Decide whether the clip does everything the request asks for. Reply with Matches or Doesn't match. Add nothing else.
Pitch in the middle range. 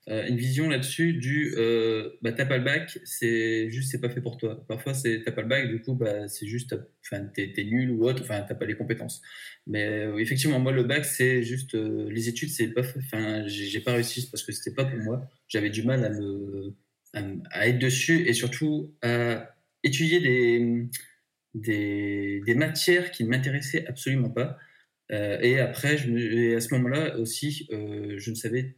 Doesn't match